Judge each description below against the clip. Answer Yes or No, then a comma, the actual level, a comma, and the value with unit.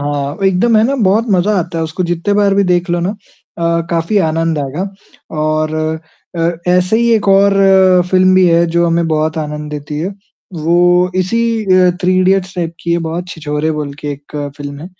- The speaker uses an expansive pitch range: No, average, 3.1 semitones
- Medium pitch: Yes, medium, 170 Hz